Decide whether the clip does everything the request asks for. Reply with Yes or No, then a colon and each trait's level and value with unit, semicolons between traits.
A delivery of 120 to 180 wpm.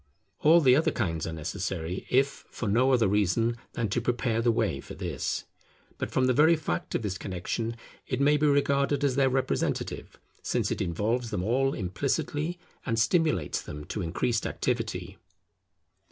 Yes: average, 170 wpm